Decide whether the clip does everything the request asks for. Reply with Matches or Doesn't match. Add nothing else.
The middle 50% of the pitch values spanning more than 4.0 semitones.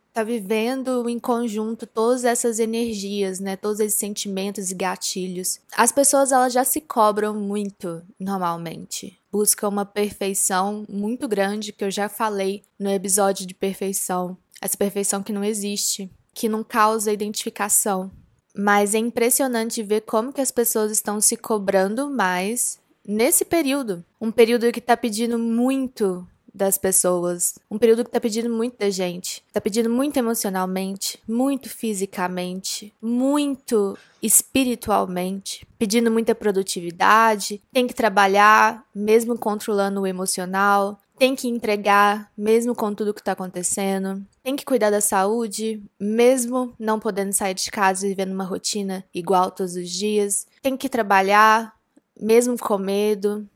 Doesn't match